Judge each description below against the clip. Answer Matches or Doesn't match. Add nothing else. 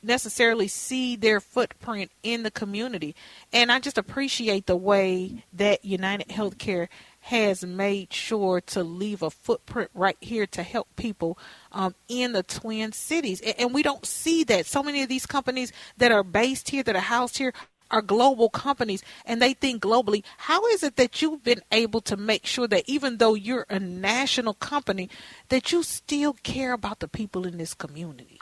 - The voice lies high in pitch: Matches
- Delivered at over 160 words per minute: Matches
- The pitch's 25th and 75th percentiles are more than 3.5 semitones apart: Matches